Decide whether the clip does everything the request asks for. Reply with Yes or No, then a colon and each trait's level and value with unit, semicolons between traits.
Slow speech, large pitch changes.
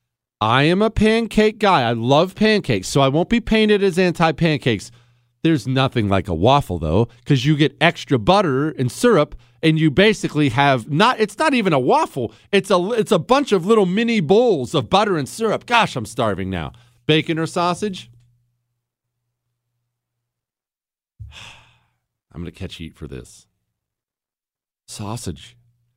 No: average, 150 wpm; wide, 8.3 semitones